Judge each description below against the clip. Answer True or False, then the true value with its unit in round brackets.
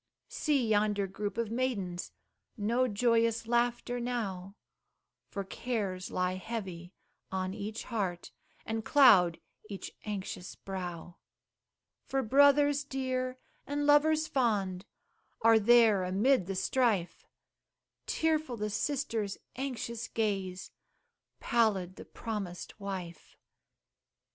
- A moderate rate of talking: False (100 wpm)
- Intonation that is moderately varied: True (4.6 semitones)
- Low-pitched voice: False (220 Hz)